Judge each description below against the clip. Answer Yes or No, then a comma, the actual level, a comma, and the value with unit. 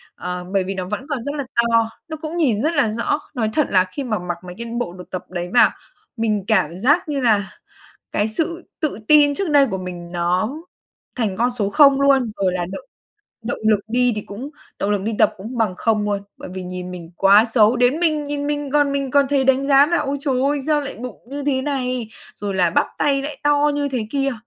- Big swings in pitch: Yes, wide, 6.1 semitones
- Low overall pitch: No, high, 245 Hz